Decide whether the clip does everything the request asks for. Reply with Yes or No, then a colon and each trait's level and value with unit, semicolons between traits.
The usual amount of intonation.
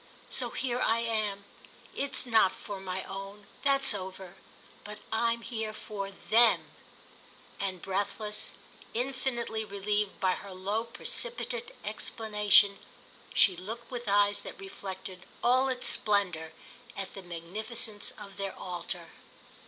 Yes: average, 3.2 semitones